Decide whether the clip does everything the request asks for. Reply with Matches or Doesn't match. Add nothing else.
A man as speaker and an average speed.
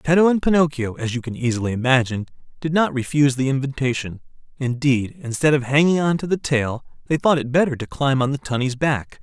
Matches